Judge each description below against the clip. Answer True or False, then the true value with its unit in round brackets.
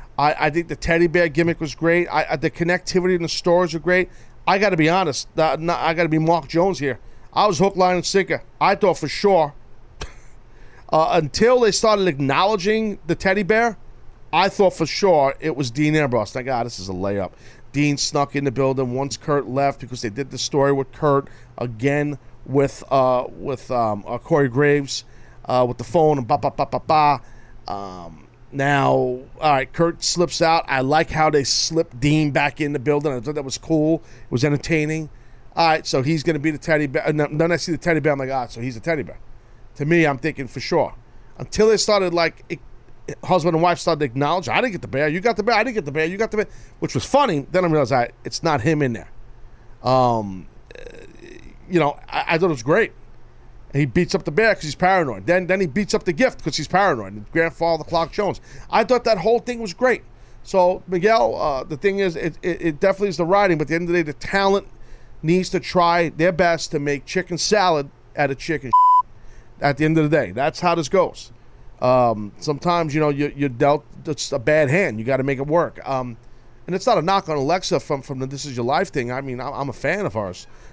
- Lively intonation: False (4.7 semitones)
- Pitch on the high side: False (155 Hz)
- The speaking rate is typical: False (235 wpm)